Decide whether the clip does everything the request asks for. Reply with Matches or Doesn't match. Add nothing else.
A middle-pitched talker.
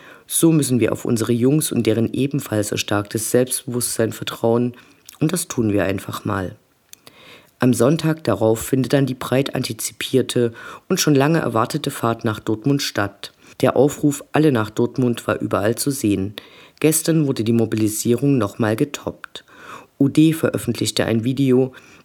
Doesn't match